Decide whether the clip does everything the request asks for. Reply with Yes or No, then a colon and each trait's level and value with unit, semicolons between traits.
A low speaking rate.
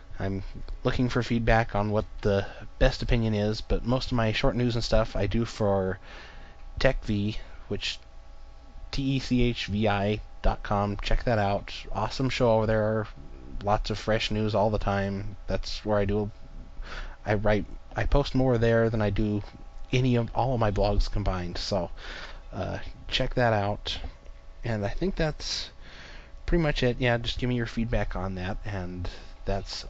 No: average, 165 wpm